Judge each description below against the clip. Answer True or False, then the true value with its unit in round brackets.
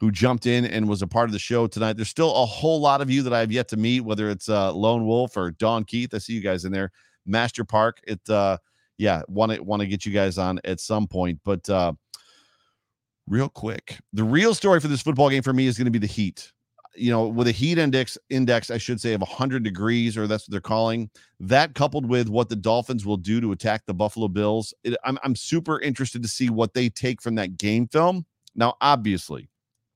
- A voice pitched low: True (115 Hz)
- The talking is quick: True (240 wpm)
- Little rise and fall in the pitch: False (3.1 semitones)